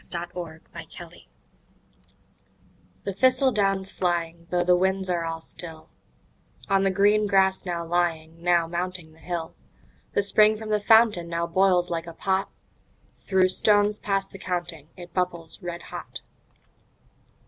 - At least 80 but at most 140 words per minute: Yes, slow, 135 wpm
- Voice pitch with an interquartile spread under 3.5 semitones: Yes, narrow, 2.5 semitones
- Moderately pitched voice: Yes, medium, 180 Hz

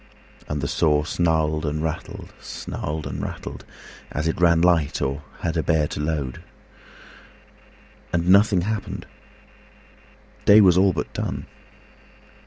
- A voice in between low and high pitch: No, very low, 80 Hz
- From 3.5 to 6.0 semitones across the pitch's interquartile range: No, average, 2.7 semitones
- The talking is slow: Yes, slow, 120 wpm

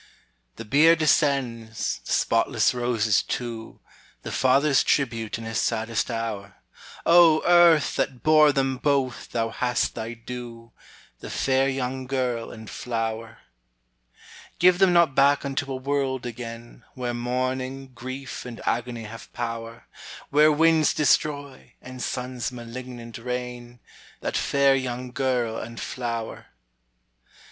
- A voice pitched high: No, low, 125 Hz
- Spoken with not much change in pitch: No, average, 3.0 semitones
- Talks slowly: Yes, slow, 125 wpm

